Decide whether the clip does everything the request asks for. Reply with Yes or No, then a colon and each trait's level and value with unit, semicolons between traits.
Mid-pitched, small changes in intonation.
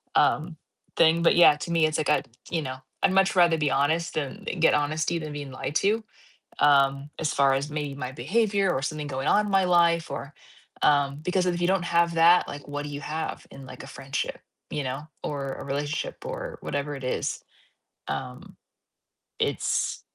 No: medium, 150 Hz; average, 3.4 semitones